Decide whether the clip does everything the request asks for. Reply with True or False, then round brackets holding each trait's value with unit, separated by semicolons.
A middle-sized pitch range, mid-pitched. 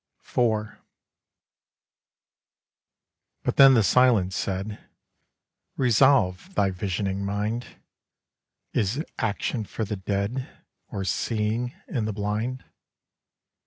False (3.8 semitones; 105 Hz)